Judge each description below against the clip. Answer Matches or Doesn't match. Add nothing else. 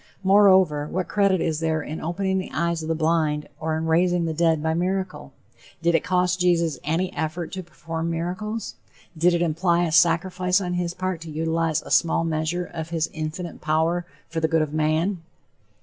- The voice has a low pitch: Doesn't match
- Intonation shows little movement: Matches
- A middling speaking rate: Matches